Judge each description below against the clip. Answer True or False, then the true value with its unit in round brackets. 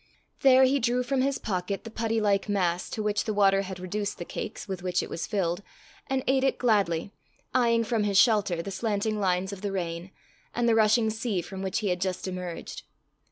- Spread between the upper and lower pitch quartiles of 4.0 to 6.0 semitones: False (3.4 semitones)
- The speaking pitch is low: False (205 Hz)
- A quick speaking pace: True (210 wpm)